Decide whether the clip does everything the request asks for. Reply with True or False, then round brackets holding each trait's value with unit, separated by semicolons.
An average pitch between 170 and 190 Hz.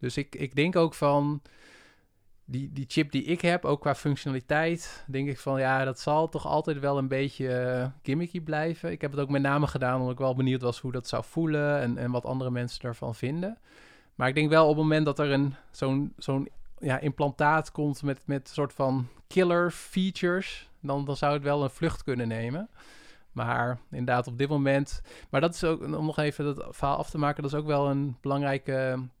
False (140 Hz)